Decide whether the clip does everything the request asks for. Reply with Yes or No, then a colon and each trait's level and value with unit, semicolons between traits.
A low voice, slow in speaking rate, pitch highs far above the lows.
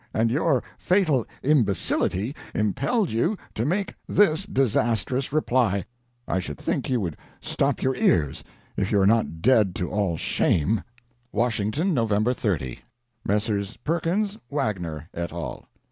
Yes: low, 115 Hz; slow, 130 wpm; wide, 6.8 semitones